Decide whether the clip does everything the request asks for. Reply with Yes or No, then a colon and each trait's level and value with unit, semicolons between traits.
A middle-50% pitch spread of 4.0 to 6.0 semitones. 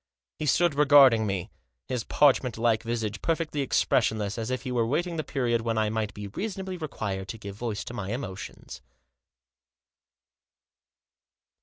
Yes: average, 4.9 semitones